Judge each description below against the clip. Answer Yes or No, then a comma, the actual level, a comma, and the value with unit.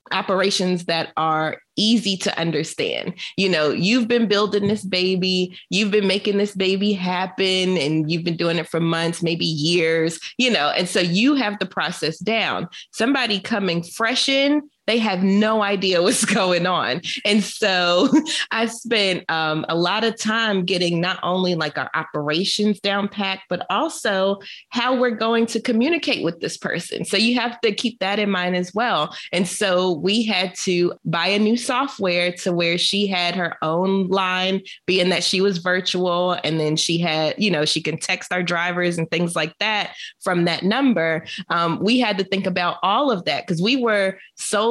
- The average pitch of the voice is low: No, high, 190 Hz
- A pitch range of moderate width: Yes, average, 3.4 semitones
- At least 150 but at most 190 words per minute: Yes, average, 185 wpm